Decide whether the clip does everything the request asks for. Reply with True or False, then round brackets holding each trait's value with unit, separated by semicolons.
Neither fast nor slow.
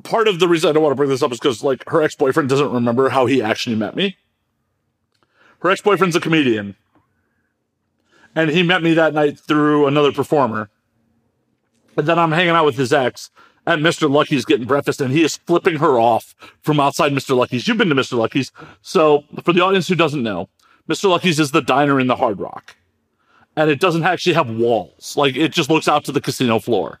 False (210 wpm)